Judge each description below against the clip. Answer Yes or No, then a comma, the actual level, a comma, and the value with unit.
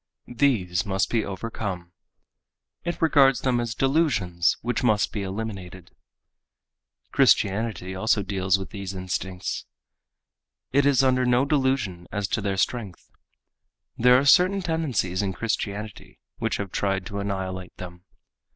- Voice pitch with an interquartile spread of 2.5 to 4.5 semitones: No, average, 5.1 semitones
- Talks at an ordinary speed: No, slow, 130 wpm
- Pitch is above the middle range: No, low, 105 Hz